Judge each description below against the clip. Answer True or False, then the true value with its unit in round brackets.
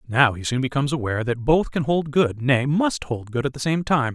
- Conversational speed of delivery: False (260 wpm)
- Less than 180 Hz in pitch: True (135 Hz)